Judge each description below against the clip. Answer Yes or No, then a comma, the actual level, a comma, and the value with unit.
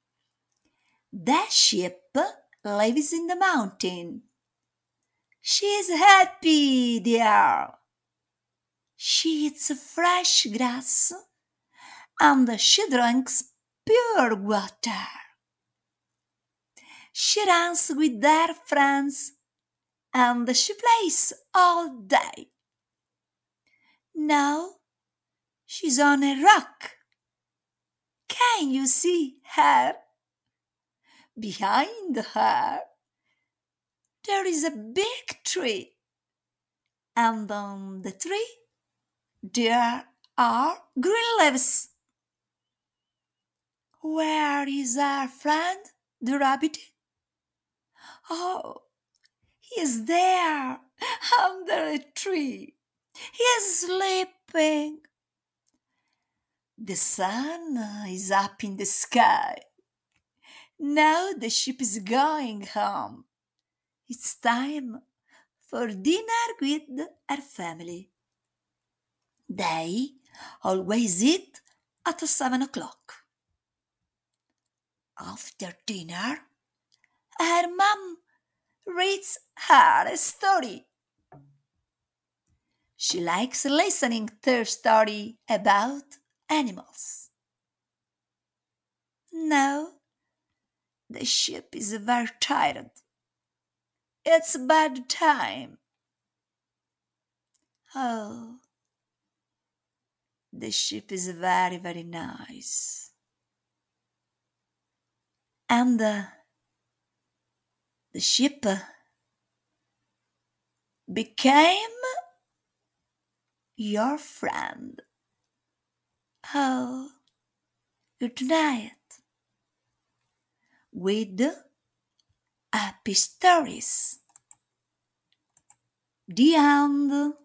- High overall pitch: Yes, very high, 285 Hz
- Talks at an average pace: No, slow, 65 wpm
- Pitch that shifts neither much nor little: No, wide, 6.6 semitones